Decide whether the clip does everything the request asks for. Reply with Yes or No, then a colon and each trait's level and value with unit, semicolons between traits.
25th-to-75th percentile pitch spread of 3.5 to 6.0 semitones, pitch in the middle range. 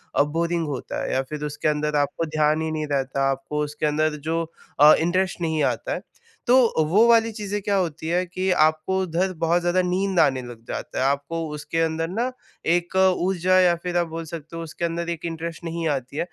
No: average, 2.8 semitones; medium, 165 Hz